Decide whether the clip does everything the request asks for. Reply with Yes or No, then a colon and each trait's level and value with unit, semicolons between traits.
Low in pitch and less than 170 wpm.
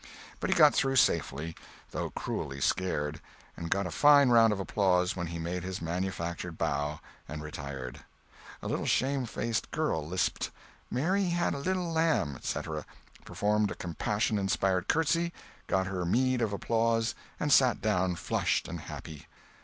Yes: very low, 95 Hz; average, 155 wpm